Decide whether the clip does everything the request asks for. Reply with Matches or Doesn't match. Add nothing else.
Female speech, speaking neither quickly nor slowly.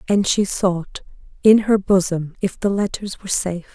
Matches